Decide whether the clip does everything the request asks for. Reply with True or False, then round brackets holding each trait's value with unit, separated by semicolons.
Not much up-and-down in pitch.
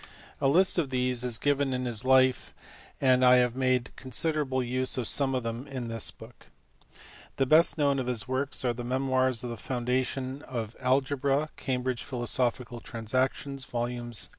True (1.6 semitones)